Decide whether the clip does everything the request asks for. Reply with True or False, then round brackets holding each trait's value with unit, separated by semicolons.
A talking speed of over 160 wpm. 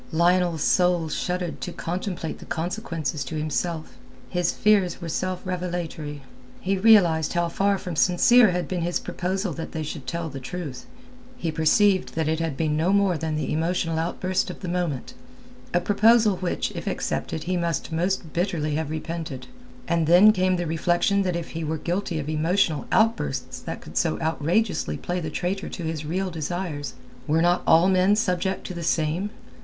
True (180 wpm)